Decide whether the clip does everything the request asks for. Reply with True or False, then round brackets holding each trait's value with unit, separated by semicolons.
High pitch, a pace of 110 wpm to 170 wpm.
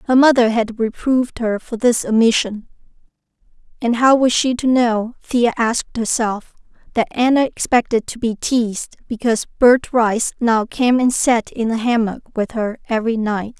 True (235 Hz; 165 wpm)